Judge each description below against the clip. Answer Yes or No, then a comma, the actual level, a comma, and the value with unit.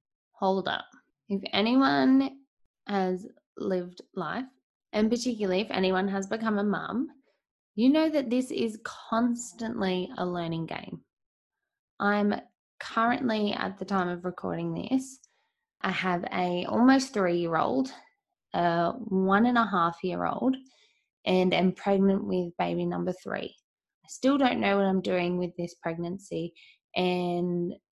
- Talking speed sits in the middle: No, slow, 130 wpm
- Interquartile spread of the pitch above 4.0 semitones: Yes, average, 5.3 semitones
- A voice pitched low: No, high, 195 Hz